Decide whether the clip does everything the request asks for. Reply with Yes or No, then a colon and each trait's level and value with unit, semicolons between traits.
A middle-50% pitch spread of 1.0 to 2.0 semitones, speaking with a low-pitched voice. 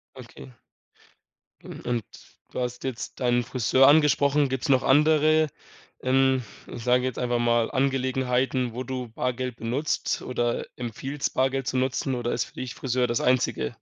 Yes: narrow, 1.6 semitones; low, 130 Hz